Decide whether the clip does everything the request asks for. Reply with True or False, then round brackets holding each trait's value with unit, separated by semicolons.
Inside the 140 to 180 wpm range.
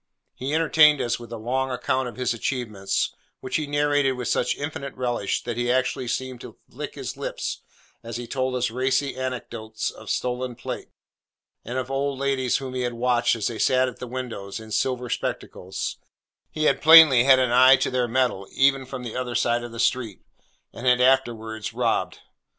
False (190 wpm)